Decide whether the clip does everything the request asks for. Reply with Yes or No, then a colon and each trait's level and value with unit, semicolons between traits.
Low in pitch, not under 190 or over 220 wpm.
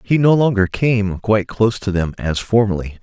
Yes: low, 105 Hz; average, 200 wpm